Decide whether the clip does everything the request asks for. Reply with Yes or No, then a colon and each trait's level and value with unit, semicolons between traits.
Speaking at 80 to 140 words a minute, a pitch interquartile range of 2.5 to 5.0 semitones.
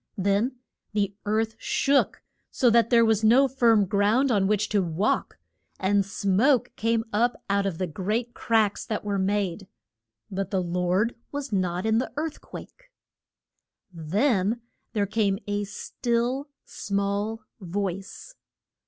Yes: slow, 135 wpm; average, 3.0 semitones